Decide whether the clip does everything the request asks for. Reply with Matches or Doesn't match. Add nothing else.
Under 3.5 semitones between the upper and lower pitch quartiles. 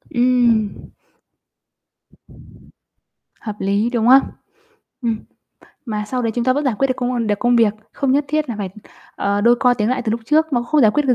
Matches